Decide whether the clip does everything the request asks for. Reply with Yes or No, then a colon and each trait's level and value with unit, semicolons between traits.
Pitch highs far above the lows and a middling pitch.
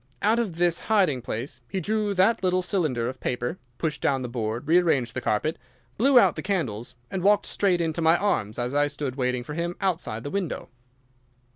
Yes: wide, 7.1 semitones; medium, 160 Hz